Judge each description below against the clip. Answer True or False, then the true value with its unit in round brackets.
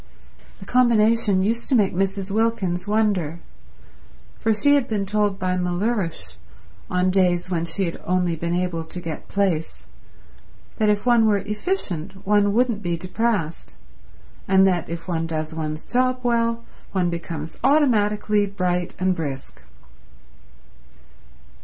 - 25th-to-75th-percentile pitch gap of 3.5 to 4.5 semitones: True (3.8 semitones)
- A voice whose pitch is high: True (195 Hz)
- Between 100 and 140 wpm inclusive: True (135 wpm)